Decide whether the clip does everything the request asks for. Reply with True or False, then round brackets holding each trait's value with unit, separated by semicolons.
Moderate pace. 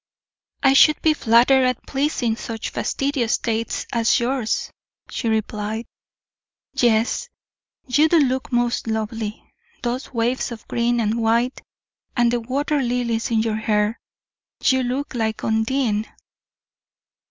False (125 wpm)